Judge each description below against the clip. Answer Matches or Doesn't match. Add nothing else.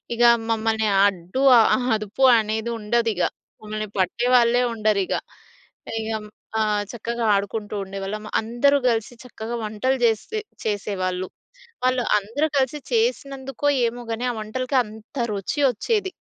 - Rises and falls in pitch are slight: Doesn't match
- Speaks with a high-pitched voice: Matches